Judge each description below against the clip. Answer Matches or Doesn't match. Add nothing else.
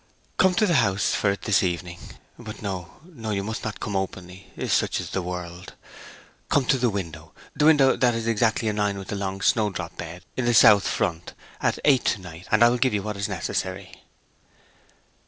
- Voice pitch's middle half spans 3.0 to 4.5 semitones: Matches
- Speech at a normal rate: Doesn't match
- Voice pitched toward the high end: Doesn't match